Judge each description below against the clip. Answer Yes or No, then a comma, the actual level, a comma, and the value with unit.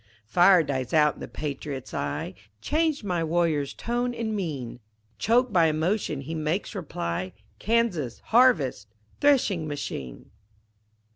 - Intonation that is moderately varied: No, wide, 7.6 semitones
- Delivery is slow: Yes, slow, 125 wpm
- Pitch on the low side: No, medium, 165 Hz